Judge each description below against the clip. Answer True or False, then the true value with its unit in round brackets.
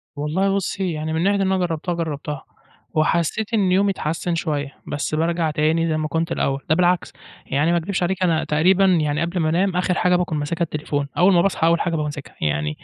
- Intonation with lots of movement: False (3.0 semitones)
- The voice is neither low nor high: True (165 Hz)